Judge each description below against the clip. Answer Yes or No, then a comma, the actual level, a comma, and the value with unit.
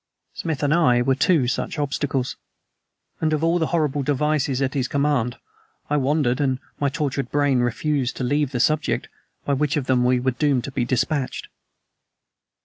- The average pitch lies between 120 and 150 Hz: Yes, medium, 140 Hz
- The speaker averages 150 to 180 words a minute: Yes, average, 175 wpm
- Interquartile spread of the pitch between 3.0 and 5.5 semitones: No, narrow, 2.6 semitones